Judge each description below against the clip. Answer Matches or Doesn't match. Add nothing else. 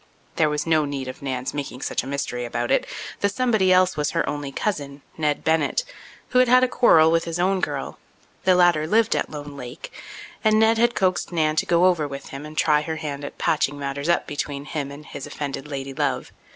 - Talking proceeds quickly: Matches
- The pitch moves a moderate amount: Matches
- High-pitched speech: Doesn't match